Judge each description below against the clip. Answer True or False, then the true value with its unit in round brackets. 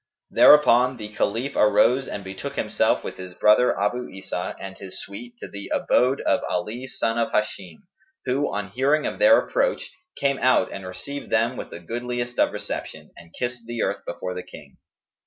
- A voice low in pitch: True (115 Hz)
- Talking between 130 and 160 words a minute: False (180 wpm)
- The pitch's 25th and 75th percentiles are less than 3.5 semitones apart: False (4.2 semitones)